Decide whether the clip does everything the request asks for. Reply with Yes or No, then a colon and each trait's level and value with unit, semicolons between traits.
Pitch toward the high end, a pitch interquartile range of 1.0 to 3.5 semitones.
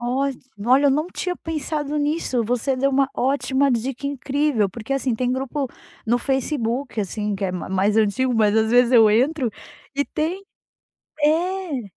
No: very high, 260 Hz; average, 4.0 semitones